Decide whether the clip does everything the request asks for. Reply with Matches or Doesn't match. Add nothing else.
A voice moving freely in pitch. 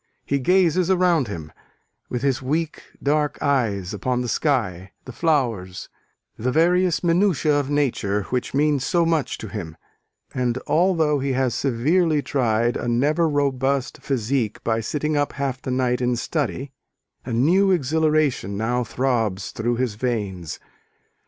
Doesn't match